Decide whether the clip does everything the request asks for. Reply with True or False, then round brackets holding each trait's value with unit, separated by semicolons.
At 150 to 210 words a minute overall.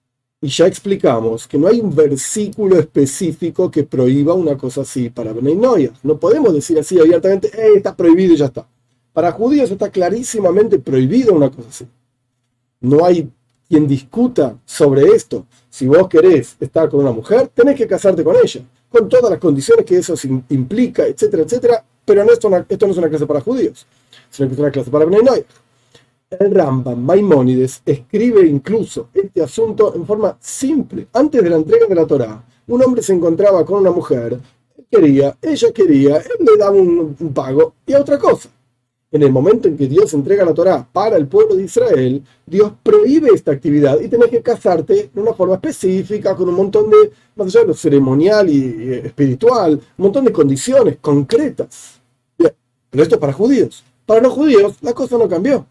True (185 wpm)